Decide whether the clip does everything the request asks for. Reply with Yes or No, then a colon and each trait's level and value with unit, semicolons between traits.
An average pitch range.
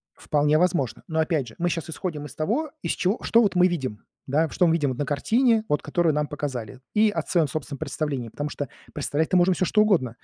Yes: average, 3.9 semitones